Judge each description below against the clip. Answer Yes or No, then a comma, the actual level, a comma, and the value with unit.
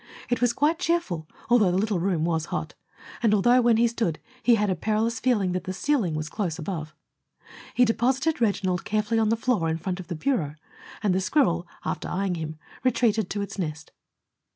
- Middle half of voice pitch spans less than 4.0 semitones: No, wide, 5.4 semitones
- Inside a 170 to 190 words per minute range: No, average, 200 wpm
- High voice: Yes, high, 205 Hz